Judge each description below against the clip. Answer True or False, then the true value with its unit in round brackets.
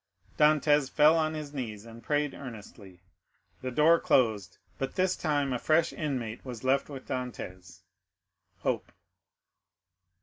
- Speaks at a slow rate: True (125 wpm)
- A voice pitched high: False (135 Hz)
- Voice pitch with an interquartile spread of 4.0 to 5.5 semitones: True (4.9 semitones)